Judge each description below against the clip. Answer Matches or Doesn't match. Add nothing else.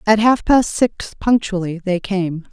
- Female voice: Matches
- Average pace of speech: Matches